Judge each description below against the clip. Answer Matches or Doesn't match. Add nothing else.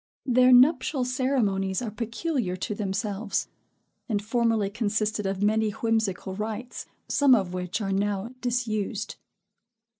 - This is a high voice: Matches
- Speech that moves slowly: Matches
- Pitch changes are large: Doesn't match